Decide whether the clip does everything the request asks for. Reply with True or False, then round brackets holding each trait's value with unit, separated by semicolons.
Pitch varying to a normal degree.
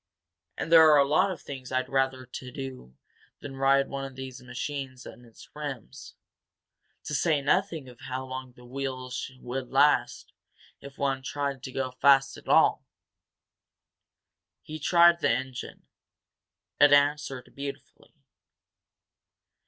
False (1.9 semitones)